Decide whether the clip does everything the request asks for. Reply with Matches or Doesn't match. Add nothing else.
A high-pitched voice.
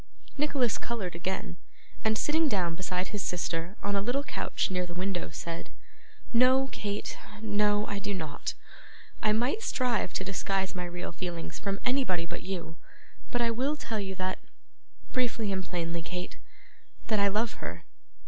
Matches